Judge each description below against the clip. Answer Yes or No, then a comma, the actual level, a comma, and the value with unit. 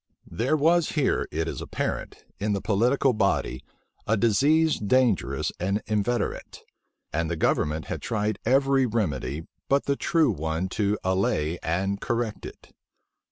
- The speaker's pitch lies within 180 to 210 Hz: No, low, 105 Hz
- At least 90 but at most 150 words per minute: Yes, average, 140 wpm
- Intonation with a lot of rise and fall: Yes, wide, 6.3 semitones